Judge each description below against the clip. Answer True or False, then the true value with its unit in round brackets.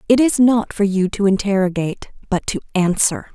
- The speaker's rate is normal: True (180 wpm)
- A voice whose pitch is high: True (205 Hz)